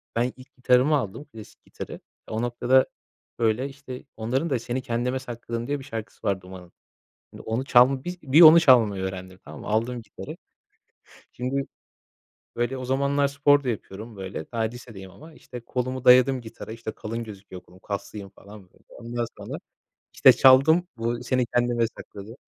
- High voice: No, low, 120 Hz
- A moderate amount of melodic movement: Yes, average, 3.2 semitones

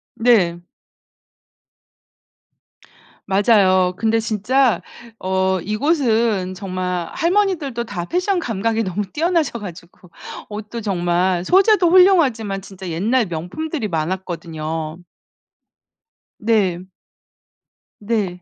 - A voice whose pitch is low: No, high, 205 Hz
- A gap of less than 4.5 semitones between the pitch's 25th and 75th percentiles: No, average, 5.1 semitones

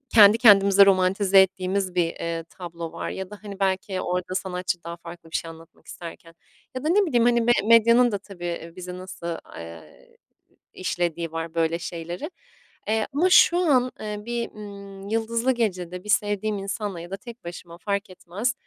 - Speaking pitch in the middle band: No, high, 195 Hz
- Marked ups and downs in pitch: No, average, 3.9 semitones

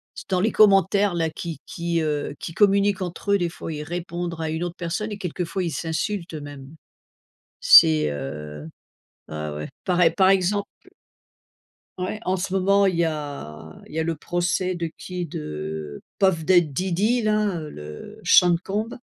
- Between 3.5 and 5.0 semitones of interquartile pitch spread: Yes, average, 4.2 semitones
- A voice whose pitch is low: No, medium, 170 Hz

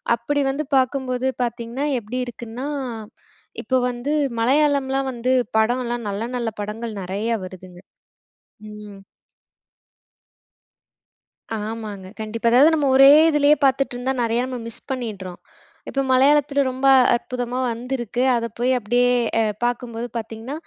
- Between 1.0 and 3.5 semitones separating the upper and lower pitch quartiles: Yes, average, 2.8 semitones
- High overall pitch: Yes, high, 245 Hz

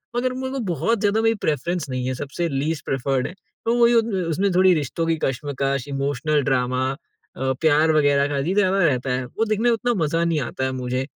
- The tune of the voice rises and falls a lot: Yes, wide, 6.5 semitones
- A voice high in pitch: No, medium, 150 Hz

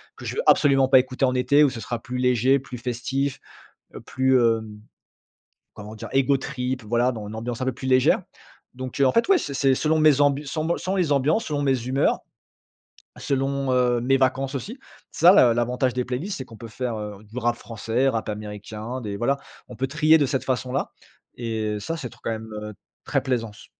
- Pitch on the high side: No, low, 130 Hz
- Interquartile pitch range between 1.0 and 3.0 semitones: Yes, average, 2.7 semitones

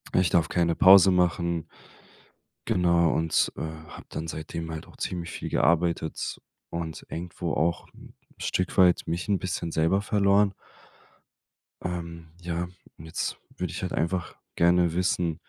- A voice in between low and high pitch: No, very low, 85 Hz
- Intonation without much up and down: Yes, narrow, 1.6 semitones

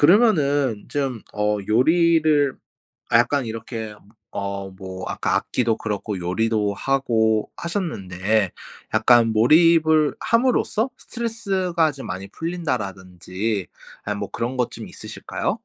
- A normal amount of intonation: No, wide, 7.5 semitones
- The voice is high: No, low, 120 Hz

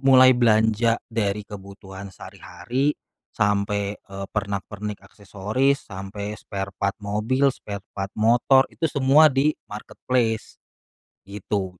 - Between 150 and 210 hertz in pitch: No, low, 105 Hz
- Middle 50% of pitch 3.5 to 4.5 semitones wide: Yes, average, 4.1 semitones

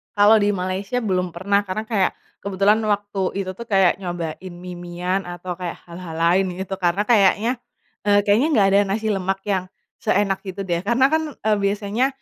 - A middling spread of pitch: No, narrow, 2.2 semitones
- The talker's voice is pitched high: Yes, high, 195 Hz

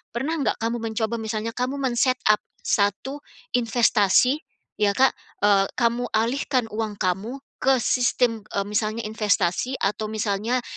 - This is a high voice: Yes, high, 225 Hz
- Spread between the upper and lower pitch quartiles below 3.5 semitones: Yes, average, 3.1 semitones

